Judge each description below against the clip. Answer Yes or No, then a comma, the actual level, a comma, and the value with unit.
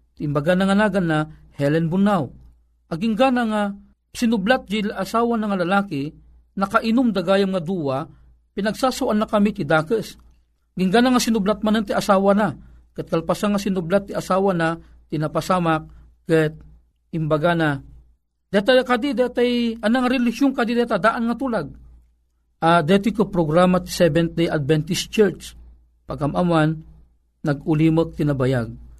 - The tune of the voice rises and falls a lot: Yes, wide, 6.0 semitones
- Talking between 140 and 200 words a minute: No, average, 130 wpm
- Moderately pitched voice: Yes, medium, 180 Hz